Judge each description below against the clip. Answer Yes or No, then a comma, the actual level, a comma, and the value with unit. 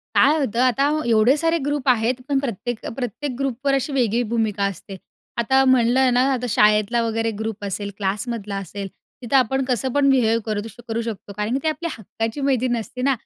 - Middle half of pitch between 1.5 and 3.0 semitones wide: No, average, 3.6 semitones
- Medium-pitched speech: No, high, 240 Hz